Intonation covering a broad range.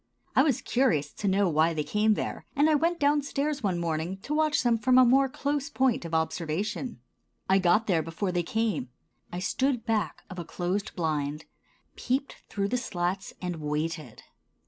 Yes: wide, 7.8 semitones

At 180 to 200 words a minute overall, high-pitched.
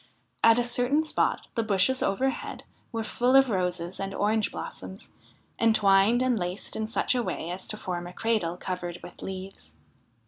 No: average, 170 wpm; high, 210 Hz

